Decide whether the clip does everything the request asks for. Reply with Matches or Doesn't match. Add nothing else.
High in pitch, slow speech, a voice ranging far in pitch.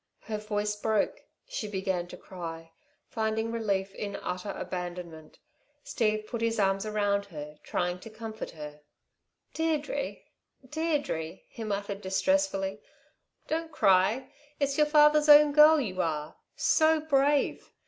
Matches